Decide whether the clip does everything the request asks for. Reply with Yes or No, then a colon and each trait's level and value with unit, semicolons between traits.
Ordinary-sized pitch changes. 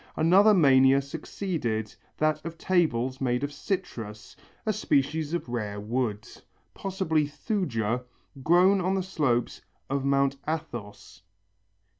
No: wide, 6.2 semitones